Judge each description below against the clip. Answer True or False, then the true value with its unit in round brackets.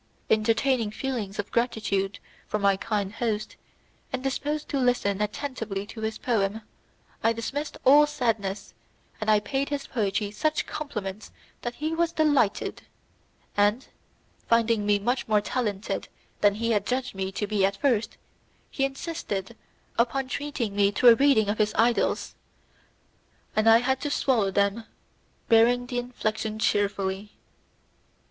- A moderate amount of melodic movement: True (3.9 semitones)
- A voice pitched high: True (225 Hz)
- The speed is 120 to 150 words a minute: True (140 wpm)